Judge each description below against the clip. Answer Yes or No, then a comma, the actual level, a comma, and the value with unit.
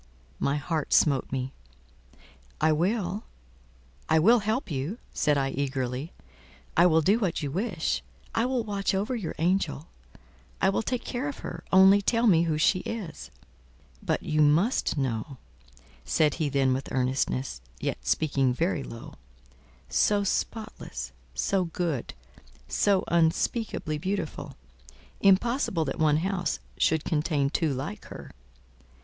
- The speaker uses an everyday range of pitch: No, wide, 6.3 semitones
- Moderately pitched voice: Yes, medium, 160 Hz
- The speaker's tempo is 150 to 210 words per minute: No, slow, 135 wpm